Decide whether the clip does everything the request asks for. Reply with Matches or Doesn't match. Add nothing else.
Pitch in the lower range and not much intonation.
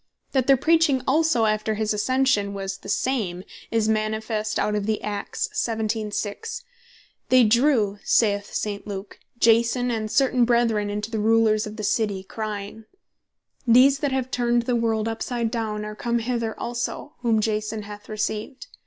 Doesn't match